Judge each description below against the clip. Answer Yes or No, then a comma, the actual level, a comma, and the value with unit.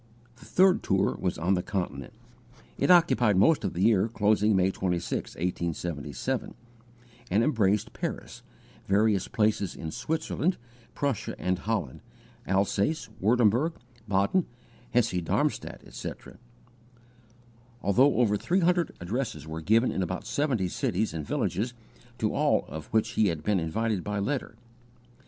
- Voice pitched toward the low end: Yes, low, 105 Hz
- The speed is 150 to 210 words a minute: No, slow, 135 wpm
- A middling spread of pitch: Yes, average, 4.9 semitones